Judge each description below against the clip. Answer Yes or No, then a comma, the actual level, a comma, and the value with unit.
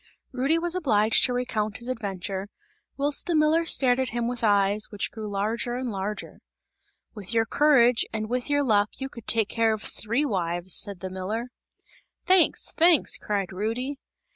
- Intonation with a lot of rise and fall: No, average, 4.4 semitones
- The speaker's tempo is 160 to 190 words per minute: Yes, average, 170 wpm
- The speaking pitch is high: Yes, high, 230 Hz